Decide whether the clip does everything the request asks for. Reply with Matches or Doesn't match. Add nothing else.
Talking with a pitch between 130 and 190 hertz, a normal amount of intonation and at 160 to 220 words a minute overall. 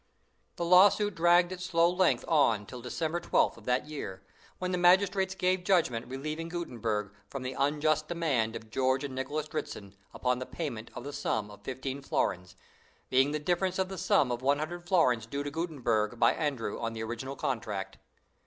Doesn't match